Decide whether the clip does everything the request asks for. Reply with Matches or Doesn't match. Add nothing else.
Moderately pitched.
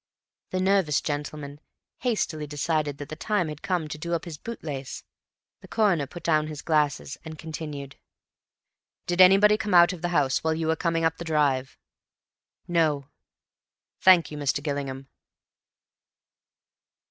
Matches